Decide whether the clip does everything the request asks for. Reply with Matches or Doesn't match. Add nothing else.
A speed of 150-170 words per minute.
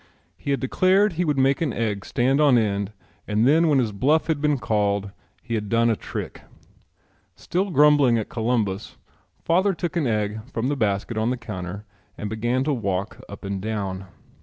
Doesn't match